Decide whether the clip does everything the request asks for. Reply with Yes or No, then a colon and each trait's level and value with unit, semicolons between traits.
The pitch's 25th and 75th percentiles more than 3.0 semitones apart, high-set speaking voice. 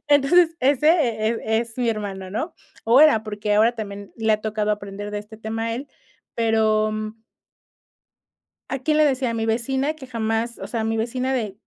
Yes: average, 3.4 semitones; high, 225 Hz